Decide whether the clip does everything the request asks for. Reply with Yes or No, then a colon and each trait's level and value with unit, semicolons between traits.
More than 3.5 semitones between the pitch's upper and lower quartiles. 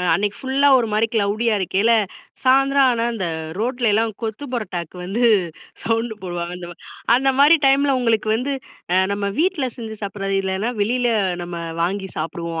Yes: average, 4.6 semitones